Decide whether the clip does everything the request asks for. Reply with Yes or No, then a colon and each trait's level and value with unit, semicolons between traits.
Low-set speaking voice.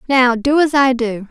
No: very high, 255 Hz